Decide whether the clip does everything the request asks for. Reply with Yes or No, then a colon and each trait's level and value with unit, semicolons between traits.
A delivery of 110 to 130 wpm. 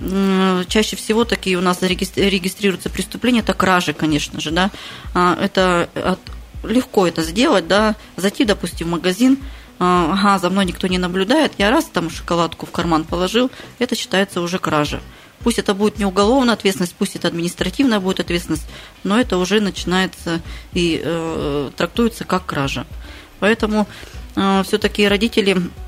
No: average, 145 wpm